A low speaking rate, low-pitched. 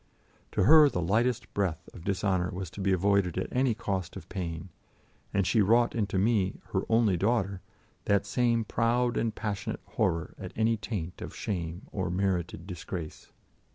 No: average, 165 wpm; low, 100 Hz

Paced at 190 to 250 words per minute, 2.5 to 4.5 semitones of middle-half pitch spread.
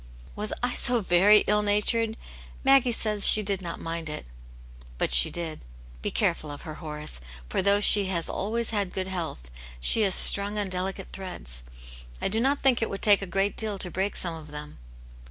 Yes: average, 195 wpm; average, 4.0 semitones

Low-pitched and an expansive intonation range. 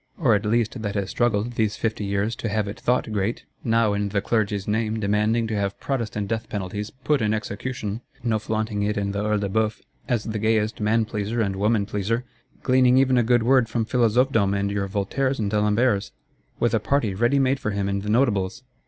No: low, 110 Hz; narrow, 2.5 semitones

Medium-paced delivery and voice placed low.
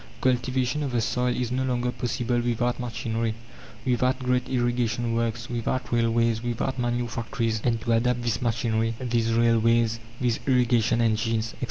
Yes: average, 155 wpm; low, 120 Hz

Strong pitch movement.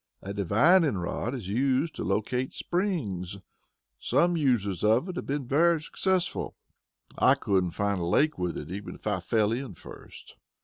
Yes: wide, 7.6 semitones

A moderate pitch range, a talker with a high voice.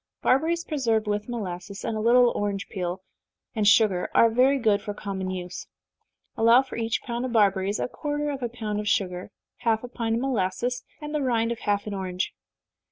Yes: average, 3.7 semitones; high, 225 Hz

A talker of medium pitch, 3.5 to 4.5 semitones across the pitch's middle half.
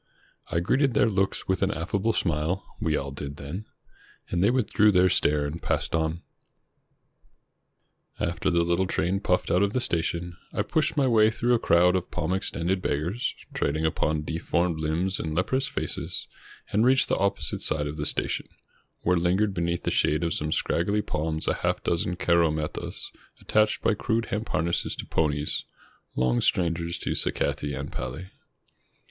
No: very low, 85 Hz; average, 4.0 semitones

